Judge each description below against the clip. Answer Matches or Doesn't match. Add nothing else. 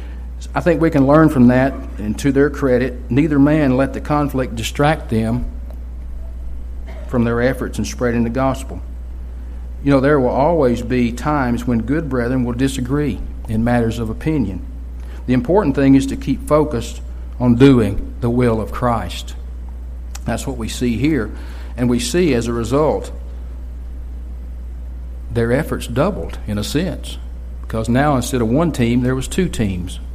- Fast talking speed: Doesn't match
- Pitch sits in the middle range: Doesn't match